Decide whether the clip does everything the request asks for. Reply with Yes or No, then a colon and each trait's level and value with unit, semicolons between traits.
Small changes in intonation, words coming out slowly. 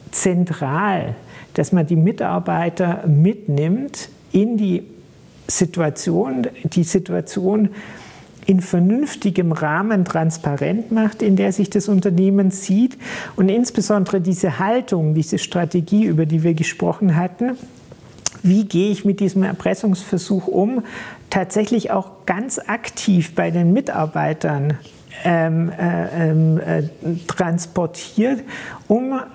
No: average, 3.6 semitones; slow, 105 wpm